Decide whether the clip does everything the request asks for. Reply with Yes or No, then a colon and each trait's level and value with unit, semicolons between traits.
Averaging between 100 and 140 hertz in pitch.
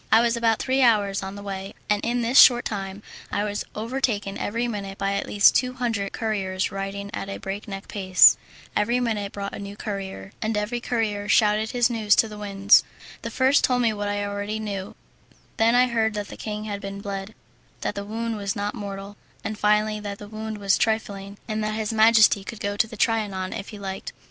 No: high, 210 Hz